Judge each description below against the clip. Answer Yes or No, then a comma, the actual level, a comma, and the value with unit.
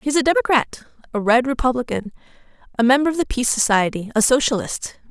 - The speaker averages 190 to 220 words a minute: No, average, 165 wpm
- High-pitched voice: Yes, high, 245 Hz